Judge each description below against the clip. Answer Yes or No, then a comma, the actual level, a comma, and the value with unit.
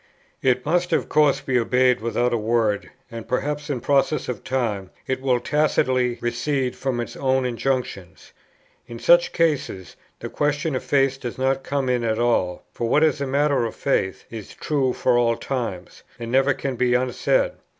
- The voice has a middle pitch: No, low, 130 Hz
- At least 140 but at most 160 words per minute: No, average, 175 wpm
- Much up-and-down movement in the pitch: No, average, 3.0 semitones